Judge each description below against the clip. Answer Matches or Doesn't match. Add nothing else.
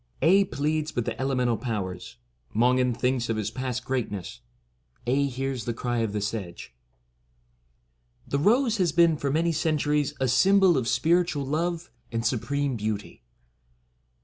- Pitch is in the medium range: Doesn't match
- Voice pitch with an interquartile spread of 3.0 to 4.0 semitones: Doesn't match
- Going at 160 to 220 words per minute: Doesn't match